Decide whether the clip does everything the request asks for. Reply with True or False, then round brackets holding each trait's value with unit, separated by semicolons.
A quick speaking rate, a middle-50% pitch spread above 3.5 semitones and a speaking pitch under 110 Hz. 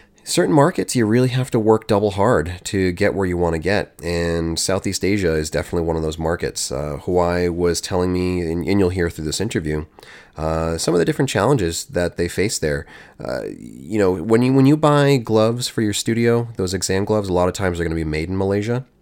True (225 wpm; 4.7 semitones; 90 Hz)